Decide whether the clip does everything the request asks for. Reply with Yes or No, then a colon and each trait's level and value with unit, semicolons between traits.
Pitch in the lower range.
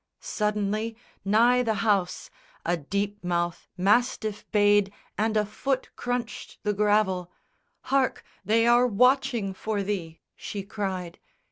No: high, 210 Hz